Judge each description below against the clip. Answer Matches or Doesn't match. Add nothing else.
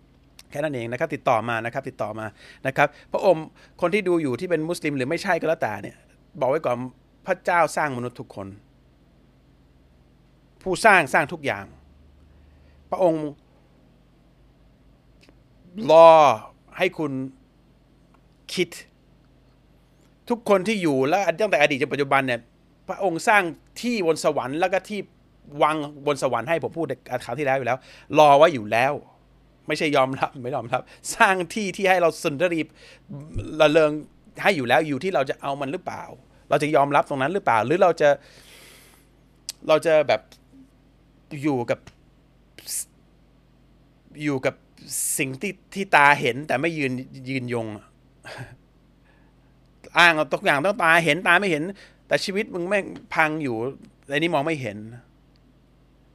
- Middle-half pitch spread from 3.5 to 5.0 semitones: Matches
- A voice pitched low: Doesn't match